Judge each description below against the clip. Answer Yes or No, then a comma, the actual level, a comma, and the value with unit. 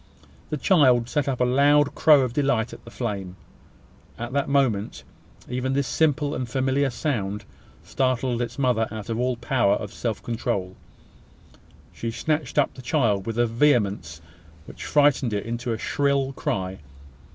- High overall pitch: No, low, 125 Hz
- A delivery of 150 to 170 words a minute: Yes, average, 160 wpm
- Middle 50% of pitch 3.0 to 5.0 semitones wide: Yes, average, 3.8 semitones